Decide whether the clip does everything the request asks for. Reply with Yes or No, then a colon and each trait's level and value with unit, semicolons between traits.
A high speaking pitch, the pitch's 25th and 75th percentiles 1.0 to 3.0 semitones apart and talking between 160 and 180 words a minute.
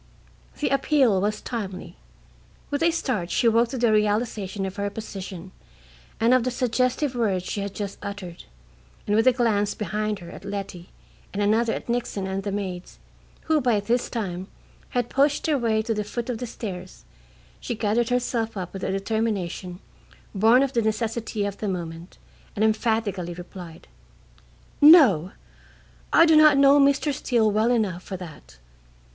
No: high, 215 Hz; average, 4.0 semitones; average, 165 wpm